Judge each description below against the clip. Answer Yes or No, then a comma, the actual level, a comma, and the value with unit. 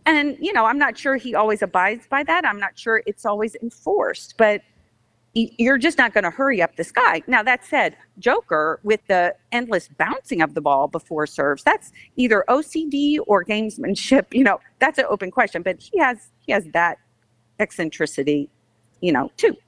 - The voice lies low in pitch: No, high, 215 Hz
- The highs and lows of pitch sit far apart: Yes, wide, 8.0 semitones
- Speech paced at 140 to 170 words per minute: No, average, 185 wpm